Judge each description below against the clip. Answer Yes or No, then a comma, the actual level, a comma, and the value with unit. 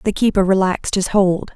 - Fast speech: No, average, 195 wpm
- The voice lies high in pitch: Yes, high, 195 Hz